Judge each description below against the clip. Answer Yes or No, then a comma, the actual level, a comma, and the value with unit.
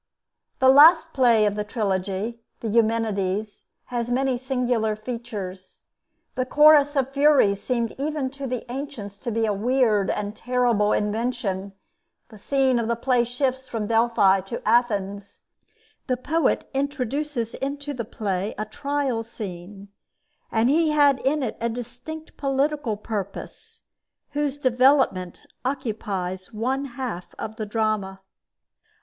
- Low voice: No, high, 235 Hz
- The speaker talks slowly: Yes, slow, 130 wpm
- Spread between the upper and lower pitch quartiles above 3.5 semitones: Yes, average, 4.3 semitones